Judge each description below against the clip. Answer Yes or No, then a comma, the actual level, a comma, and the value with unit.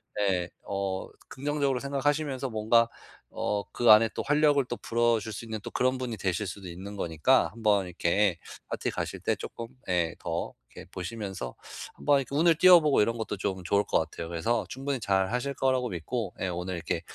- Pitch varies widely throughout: Yes, wide, 5.7 semitones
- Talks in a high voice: No, low, 110 Hz